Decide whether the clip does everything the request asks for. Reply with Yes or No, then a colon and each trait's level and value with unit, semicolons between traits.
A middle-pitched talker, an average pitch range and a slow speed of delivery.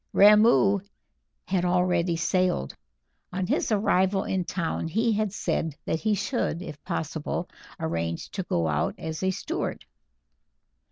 Yes: medium, 180 Hz; average, 3.8 semitones; slow, 130 wpm